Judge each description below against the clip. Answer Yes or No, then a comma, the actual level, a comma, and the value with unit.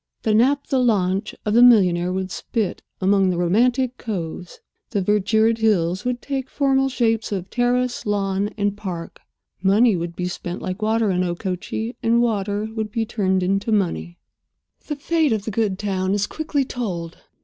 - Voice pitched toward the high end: Yes, high, 210 Hz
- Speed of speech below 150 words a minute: No, average, 165 wpm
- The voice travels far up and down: No, average, 4.1 semitones